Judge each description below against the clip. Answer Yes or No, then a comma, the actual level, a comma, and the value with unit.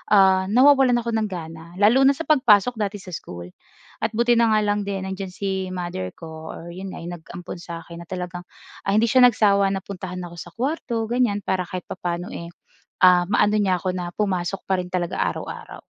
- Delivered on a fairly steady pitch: No, average, 3.5 semitones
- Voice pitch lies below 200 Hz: Yes, high, 190 Hz